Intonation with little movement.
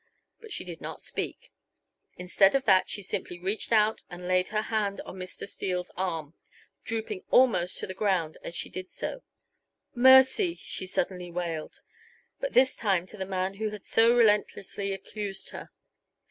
No: average, 3.2 semitones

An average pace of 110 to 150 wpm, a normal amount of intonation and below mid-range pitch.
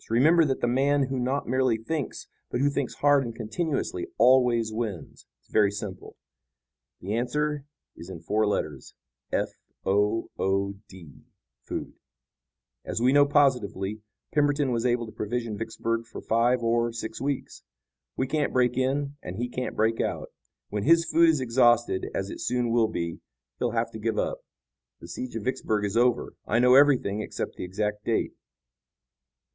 No: average, 165 wpm; average, 3.8 semitones; low, 120 Hz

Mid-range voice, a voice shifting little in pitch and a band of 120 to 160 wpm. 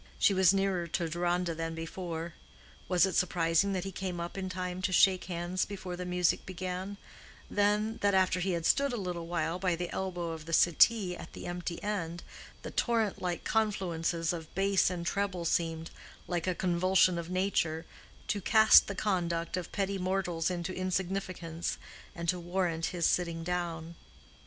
No: medium, 180 Hz; narrow, 2.0 semitones; average, 170 wpm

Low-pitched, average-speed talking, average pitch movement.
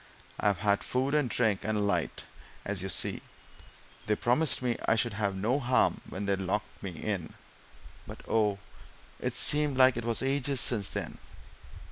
Yes: low, 110 Hz; average, 170 wpm; average, 4.1 semitones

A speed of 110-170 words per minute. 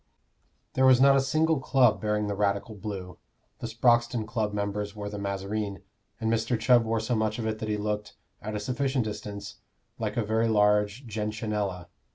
No: average, 185 wpm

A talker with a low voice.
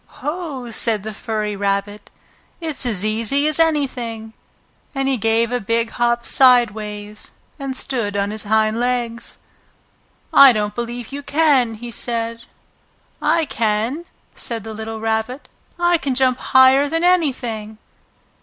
No: high, 235 Hz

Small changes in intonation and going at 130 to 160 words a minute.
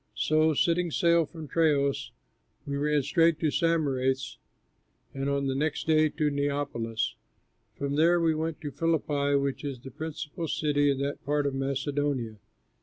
Yes: narrow, 2.3 semitones; average, 155 wpm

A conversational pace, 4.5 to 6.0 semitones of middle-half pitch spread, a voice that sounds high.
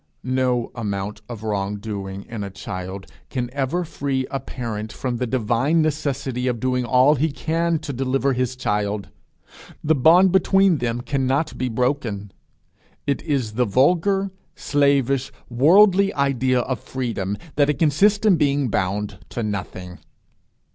No: average, 145 wpm; average, 4.9 semitones; low, 130 Hz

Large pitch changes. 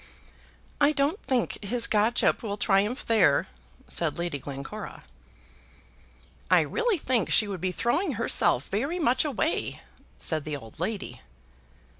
Yes: wide, 6.8 semitones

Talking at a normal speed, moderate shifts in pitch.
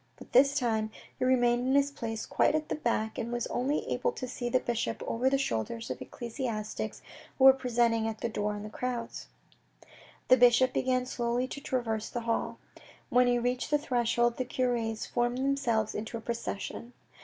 No: average, 185 wpm; narrow, 2.0 semitones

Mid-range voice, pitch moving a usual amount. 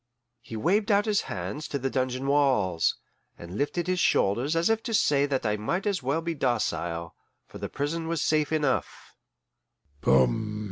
No: medium, 145 Hz; wide, 5.9 semitones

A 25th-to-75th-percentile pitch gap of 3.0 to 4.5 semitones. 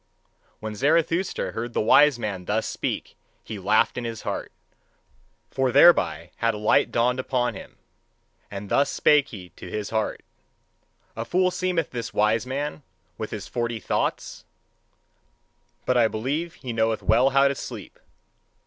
Yes: average, 4.2 semitones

